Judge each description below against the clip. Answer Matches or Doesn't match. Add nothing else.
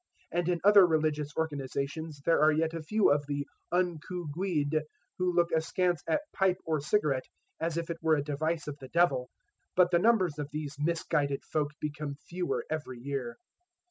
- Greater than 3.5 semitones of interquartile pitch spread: Doesn't match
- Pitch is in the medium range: Matches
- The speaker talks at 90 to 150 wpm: Doesn't match